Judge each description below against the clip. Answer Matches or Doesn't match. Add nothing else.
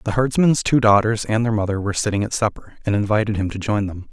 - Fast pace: Matches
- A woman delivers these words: Doesn't match